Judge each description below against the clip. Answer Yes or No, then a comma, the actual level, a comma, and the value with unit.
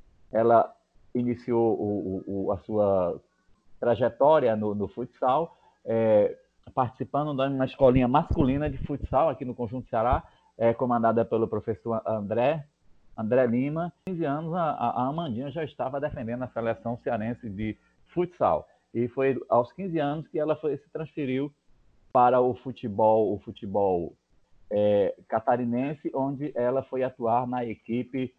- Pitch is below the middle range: Yes, low, 120 Hz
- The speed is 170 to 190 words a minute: No, average, 140 wpm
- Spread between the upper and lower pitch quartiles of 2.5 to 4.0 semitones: Yes, average, 3.6 semitones